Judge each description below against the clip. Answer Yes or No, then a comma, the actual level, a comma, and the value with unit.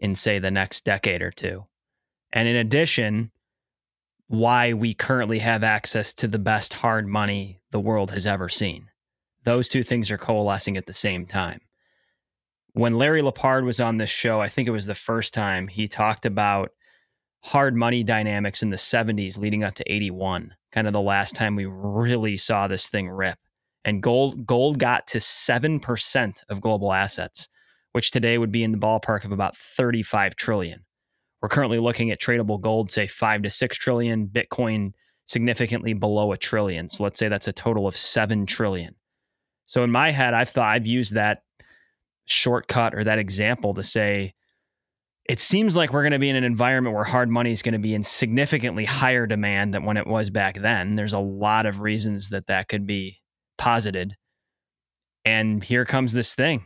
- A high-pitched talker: No, low, 110 Hz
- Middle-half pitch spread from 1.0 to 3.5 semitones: Yes, average, 2.8 semitones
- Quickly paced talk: No, average, 185 wpm